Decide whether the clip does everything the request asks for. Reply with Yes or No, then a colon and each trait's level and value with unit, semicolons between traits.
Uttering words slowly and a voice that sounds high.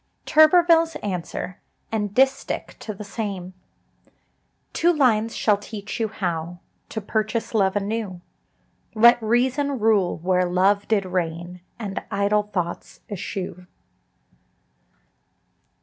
Yes: slow, 115 wpm; high, 205 Hz